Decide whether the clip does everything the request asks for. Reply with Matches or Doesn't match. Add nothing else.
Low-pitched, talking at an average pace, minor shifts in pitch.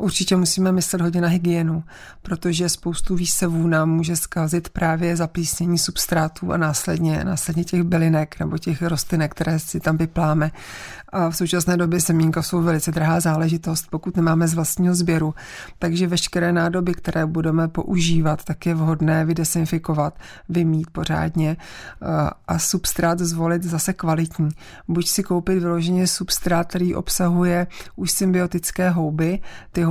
Doesn't match